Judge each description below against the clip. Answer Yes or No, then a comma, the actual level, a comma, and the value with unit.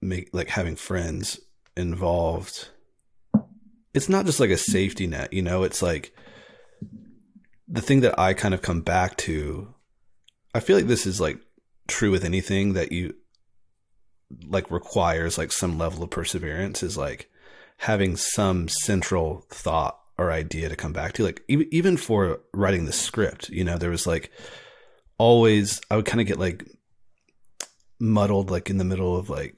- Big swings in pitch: No, average, 3.7 semitones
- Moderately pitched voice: No, very low, 95 Hz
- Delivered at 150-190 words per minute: Yes, average, 165 wpm